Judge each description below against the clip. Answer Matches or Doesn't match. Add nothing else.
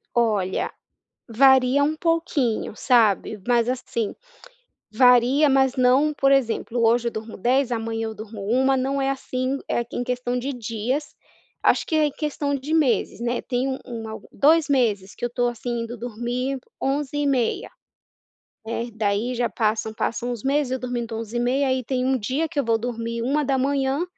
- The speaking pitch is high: Matches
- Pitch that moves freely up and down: Doesn't match